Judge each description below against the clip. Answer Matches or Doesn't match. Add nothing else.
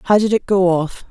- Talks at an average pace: Doesn't match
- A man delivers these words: Doesn't match